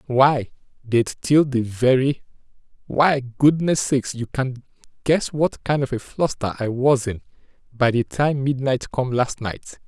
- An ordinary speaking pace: Yes, average, 160 wpm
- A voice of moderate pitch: No, low, 130 Hz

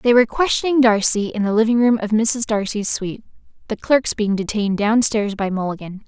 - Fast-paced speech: No, average, 190 wpm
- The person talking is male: No, female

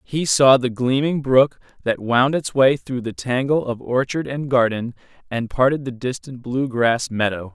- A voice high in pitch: No, low, 130 Hz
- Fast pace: No, average, 185 wpm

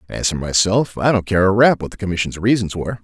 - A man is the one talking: Yes, male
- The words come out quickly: Yes, fast, 255 wpm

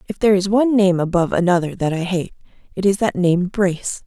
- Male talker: No, female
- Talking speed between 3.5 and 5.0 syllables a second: No, 6.3 syllables/s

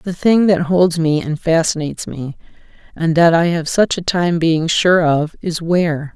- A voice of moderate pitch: Yes, medium, 165 Hz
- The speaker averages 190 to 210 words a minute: Yes, average, 195 wpm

